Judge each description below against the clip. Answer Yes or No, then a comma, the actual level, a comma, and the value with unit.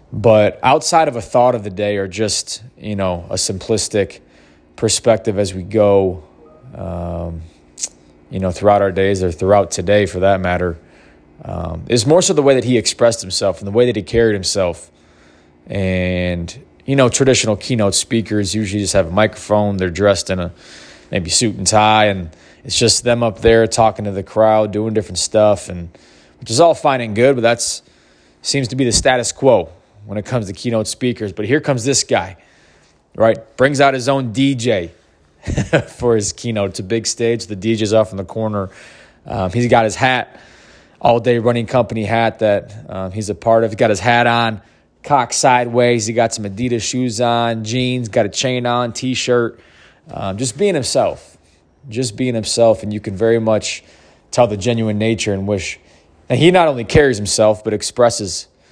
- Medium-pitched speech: No, low, 110 Hz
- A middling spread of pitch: Yes, average, 4.0 semitones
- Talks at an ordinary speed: Yes, average, 190 wpm